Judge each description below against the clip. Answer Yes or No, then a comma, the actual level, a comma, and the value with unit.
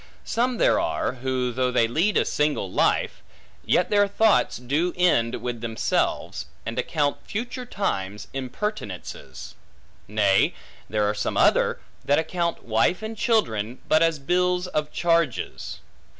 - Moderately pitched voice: Yes, medium, 145 Hz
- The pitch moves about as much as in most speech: No, wide, 7.7 semitones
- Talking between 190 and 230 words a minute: No, slow, 135 wpm